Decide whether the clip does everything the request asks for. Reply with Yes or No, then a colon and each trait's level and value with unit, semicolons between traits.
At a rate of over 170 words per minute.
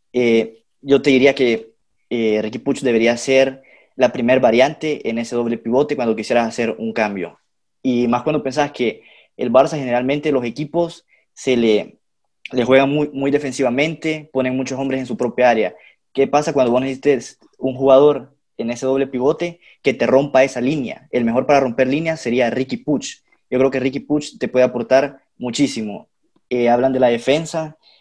Yes: average, 180 wpm